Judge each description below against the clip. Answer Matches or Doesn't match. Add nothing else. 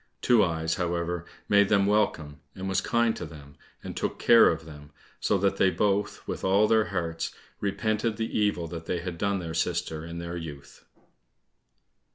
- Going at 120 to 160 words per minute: Doesn't match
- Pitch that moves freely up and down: Doesn't match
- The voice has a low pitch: Matches